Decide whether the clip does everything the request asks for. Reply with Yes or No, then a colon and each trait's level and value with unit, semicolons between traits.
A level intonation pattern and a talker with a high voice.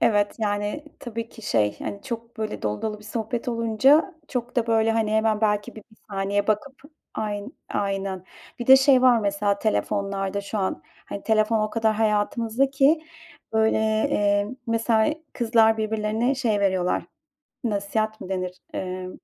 Yes: narrow, 2.2 semitones; high, 220 Hz